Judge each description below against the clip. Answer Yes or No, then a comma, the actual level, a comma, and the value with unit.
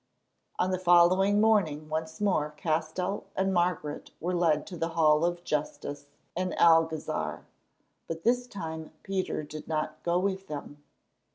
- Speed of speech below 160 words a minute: Yes, average, 150 wpm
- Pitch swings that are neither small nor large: Yes, average, 3.1 semitones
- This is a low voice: No, medium, 170 Hz